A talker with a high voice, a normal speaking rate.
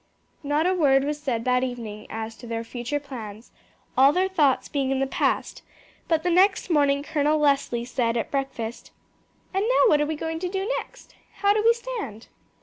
Yes: very high, 285 Hz; average, 195 wpm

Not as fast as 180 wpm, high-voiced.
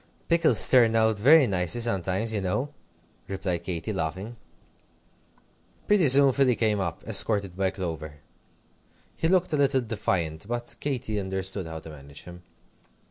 No: average, 140 wpm; low, 100 Hz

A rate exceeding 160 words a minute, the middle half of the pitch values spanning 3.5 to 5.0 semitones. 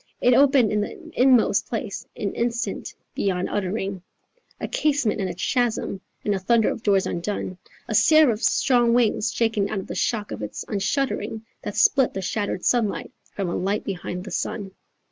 Yes: average, 170 wpm; average, 3.8 semitones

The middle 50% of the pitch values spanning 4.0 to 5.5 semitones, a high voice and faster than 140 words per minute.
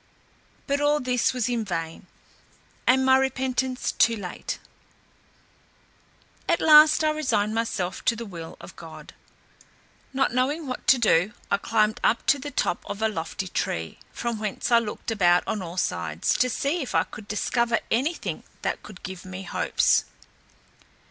Yes: average, 4.7 semitones; high, 230 Hz; average, 160 wpm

